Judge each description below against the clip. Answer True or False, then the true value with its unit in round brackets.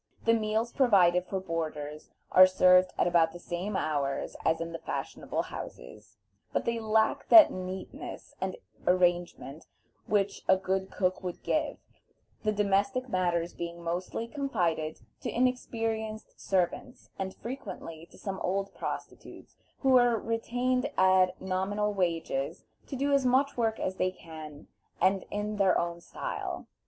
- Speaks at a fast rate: False (145 wpm)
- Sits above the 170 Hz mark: True (190 Hz)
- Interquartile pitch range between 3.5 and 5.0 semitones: True (4.3 semitones)